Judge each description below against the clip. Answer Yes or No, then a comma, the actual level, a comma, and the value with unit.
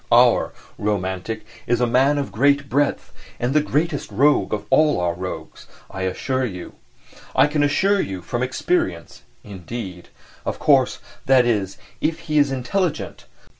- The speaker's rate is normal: Yes, average, 150 wpm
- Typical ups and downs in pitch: No, wide, 6.9 semitones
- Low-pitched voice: Yes, low, 125 Hz